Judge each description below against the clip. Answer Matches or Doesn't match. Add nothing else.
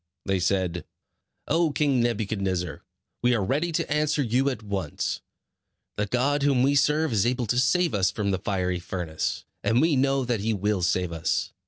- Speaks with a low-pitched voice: Matches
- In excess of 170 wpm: Matches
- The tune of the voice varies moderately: Doesn't match